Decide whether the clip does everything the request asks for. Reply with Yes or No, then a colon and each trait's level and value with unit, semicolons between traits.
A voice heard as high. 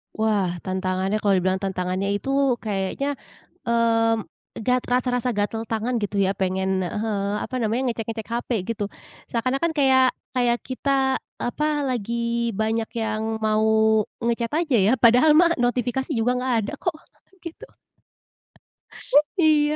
Yes: high, 225 Hz